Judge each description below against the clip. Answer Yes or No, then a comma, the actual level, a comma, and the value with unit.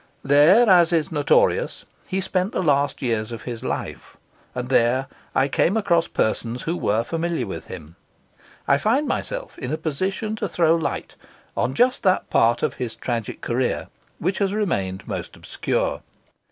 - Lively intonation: Yes, wide, 7.6 semitones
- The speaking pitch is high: No, medium, 155 Hz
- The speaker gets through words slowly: No, average, 165 wpm